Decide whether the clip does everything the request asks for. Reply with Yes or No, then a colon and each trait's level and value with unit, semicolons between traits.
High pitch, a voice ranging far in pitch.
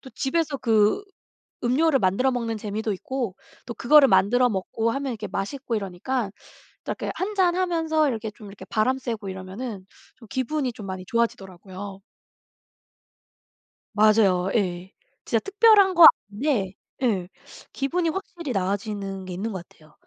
Yes: high, 225 Hz; wide, 5.7 semitones